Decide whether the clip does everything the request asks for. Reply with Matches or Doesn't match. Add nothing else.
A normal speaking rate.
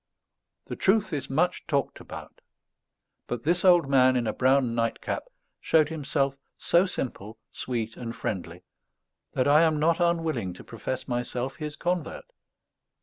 Matches